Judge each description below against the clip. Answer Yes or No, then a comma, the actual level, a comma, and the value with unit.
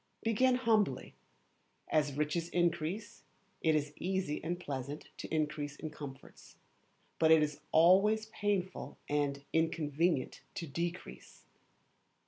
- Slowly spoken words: Yes, slow, 110 wpm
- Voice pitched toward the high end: No, medium, 160 Hz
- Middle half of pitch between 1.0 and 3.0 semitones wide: No, average, 4.2 semitones